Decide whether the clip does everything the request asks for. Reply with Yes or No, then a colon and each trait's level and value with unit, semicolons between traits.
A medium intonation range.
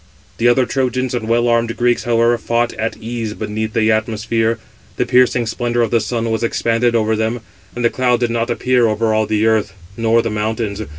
No: narrow, 1.4 semitones